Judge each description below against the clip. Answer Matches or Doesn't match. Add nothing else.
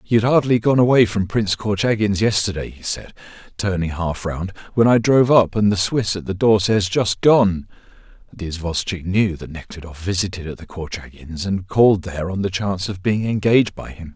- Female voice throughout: Doesn't match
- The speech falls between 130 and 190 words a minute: Doesn't match